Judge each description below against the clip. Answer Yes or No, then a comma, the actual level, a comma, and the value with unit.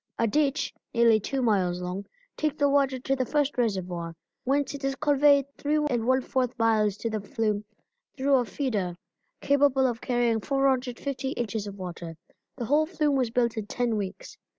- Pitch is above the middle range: Yes, high, 245 Hz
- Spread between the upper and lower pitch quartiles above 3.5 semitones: Yes, average, 4.4 semitones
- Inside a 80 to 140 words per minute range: No, average, 170 wpm